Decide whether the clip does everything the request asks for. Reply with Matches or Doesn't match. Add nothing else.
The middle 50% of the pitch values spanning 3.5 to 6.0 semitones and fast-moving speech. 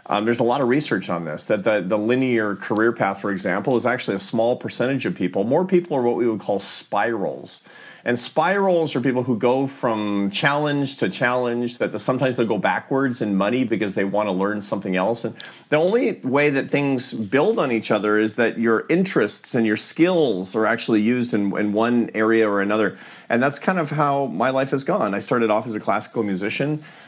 Matches